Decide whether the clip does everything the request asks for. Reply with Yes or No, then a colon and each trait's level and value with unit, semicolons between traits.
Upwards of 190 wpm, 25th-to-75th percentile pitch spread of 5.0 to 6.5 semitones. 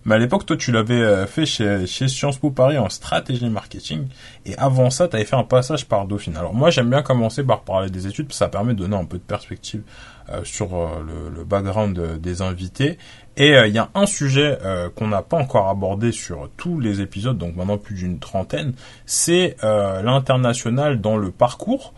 Yes: average, 215 wpm; average, 5.3 semitones